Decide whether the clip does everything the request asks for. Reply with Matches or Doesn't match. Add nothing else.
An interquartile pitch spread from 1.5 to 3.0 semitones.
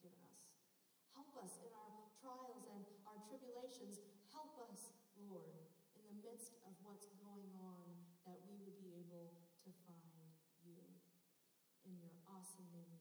Doesn't match